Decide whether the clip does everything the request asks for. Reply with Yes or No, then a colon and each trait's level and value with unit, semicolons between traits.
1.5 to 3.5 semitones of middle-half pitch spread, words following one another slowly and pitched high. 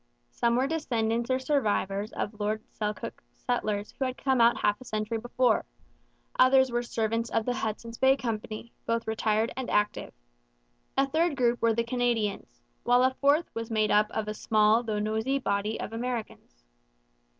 No: average, 2.9 semitones; average, 170 wpm; high, 230 Hz